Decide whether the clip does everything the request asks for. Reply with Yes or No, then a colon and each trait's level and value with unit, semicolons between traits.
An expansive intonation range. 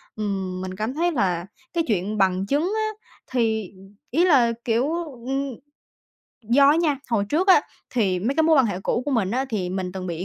Yes: wide, 6.8 semitones